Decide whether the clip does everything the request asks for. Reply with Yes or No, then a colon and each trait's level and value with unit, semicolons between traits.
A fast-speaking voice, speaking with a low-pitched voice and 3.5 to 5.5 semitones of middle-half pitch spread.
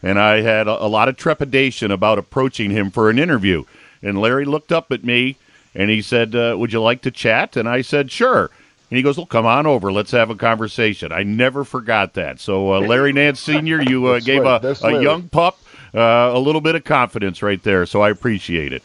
Yes: fast, 230 wpm; low, 120 Hz; average, 4.3 semitones